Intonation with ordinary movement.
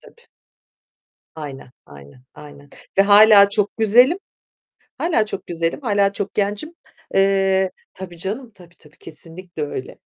Yes: average, 4.2 semitones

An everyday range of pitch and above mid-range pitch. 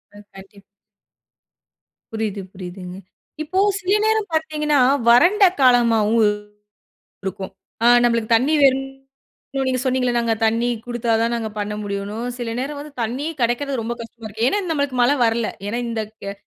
Yes: average, 3.6 semitones; high, 235 Hz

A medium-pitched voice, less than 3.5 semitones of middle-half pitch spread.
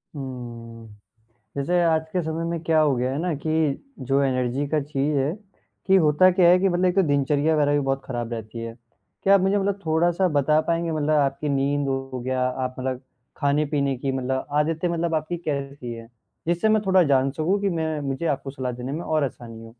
No: medium, 145 Hz; average, 3.9 semitones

